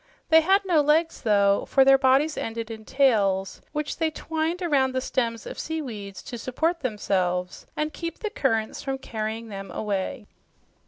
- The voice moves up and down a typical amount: No, wide, 6.2 semitones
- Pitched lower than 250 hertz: No, very high, 260 Hz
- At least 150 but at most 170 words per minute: Yes, average, 165 wpm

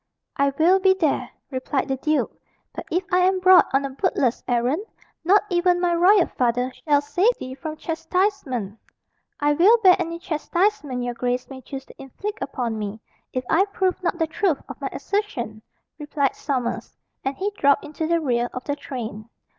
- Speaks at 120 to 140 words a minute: No, average, 180 wpm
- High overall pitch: Yes, very high, 300 Hz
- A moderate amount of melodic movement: No, wide, 6.0 semitones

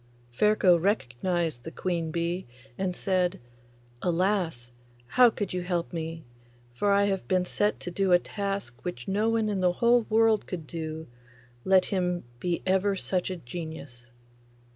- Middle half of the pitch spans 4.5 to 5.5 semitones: No, average, 3.2 semitones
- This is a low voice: No, medium, 180 Hz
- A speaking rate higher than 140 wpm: Yes, average, 155 wpm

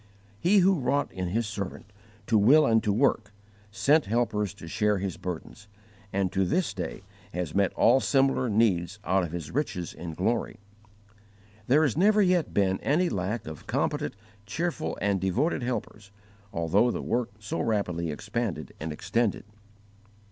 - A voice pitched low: Yes, low, 105 Hz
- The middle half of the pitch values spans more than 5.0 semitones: Yes, wide, 5.5 semitones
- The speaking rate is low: No, average, 155 wpm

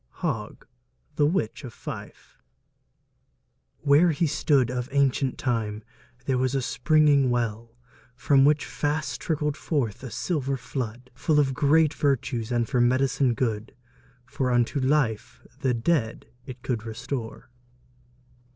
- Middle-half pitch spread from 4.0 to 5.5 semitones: No, average, 3.3 semitones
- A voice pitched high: No, low, 130 Hz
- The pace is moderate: No, slow, 130 wpm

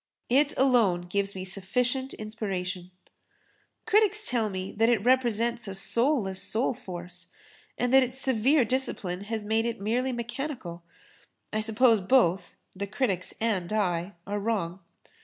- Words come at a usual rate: No, slow, 130 wpm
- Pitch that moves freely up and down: No, average, 4.8 semitones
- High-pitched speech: Yes, high, 220 Hz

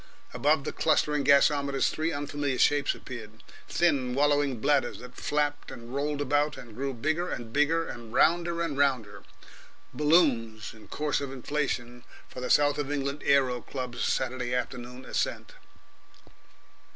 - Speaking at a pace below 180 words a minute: Yes, average, 140 wpm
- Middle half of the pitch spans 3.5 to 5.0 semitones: No, average, 2.8 semitones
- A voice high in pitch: No, medium, 140 Hz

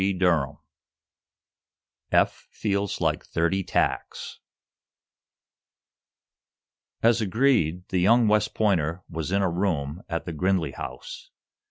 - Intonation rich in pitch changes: No, average, 3.6 semitones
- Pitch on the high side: No, very low, 95 Hz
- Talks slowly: Yes, slow, 110 wpm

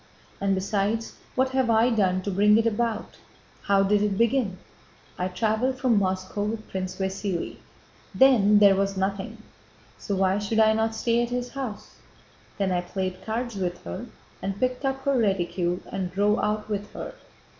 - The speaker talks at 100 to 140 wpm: No, average, 170 wpm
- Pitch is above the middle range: Yes, high, 205 Hz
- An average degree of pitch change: Yes, average, 3.1 semitones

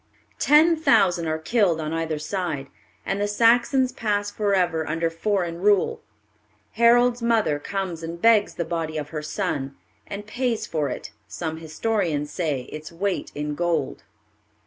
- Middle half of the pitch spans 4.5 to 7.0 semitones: Yes, average, 5.2 semitones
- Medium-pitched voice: Yes, medium, 175 Hz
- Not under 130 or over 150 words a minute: Yes, average, 145 wpm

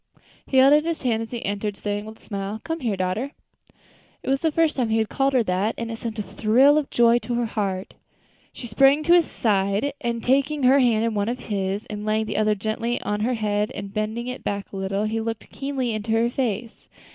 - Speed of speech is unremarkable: No, fast, 240 wpm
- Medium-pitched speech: No, high, 225 Hz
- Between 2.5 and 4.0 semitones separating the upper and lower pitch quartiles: Yes, average, 3.6 semitones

